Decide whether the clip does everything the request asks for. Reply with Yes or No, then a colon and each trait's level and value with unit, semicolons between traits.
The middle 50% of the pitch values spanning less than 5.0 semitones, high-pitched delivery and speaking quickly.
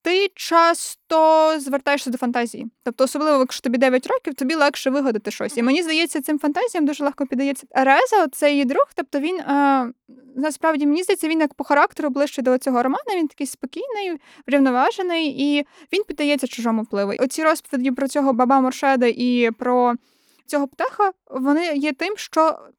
Yes: average, 3.4 semitones; very high, 285 Hz; fast, 165 wpm